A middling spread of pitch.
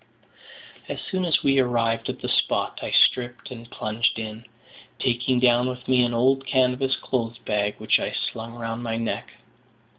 No: narrow, 1.9 semitones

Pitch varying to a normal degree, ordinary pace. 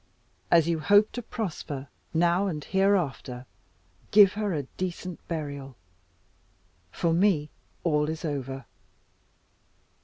No: average, 4.7 semitones; slow, 110 wpm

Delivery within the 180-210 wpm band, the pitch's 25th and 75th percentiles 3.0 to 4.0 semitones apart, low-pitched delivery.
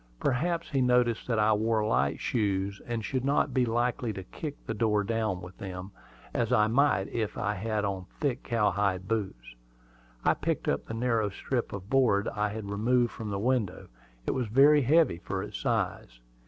Yes: average, 185 wpm; average, 3.6 semitones; low, 110 Hz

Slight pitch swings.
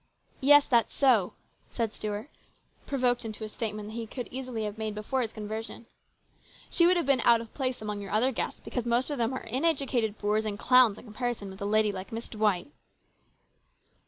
No: average, 3.2 semitones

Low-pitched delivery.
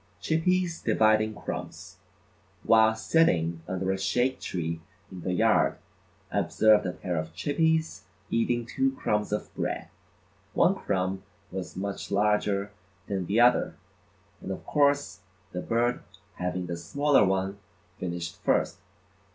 Yes: low, 100 Hz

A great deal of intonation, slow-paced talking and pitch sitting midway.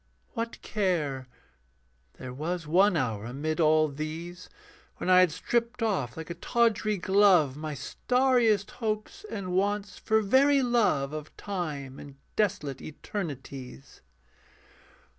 Yes: wide, 6.2 semitones; slow, 120 wpm; medium, 180 Hz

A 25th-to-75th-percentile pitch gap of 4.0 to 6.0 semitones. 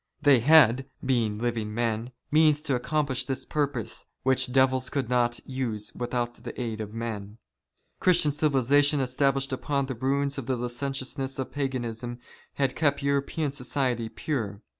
No: average, 2.8 semitones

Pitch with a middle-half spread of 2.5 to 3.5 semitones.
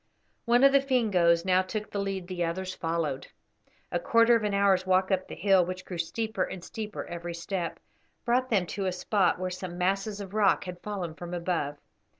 Yes: average, 2.9 semitones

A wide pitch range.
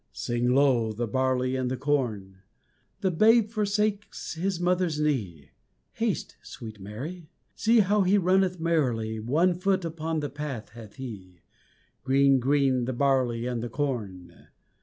Yes: wide, 6.9 semitones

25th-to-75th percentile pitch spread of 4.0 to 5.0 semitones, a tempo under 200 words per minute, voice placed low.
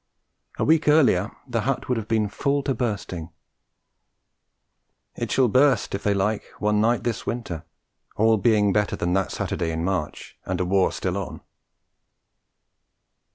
Yes: average, 4.3 semitones; average, 155 wpm; low, 105 Hz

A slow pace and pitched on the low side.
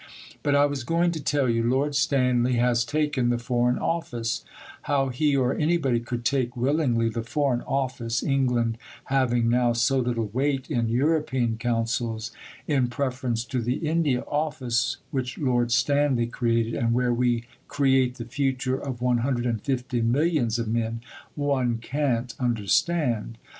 No: average, 145 wpm; low, 125 Hz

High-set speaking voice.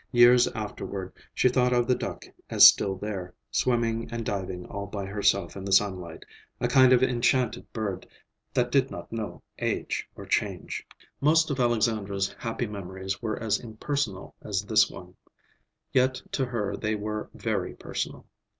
No: low, 110 Hz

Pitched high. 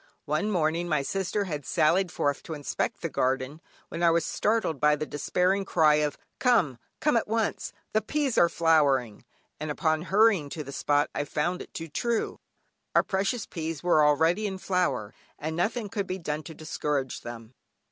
No: medium, 160 Hz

